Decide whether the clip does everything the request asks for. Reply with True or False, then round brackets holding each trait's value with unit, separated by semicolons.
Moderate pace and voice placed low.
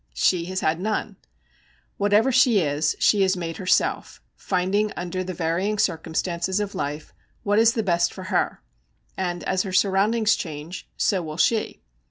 False (160 wpm; 185 Hz)